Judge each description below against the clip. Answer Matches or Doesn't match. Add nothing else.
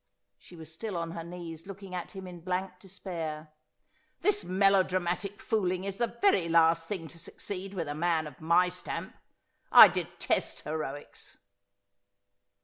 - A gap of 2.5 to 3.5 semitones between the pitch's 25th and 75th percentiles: Matches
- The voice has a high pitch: Doesn't match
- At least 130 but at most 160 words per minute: Matches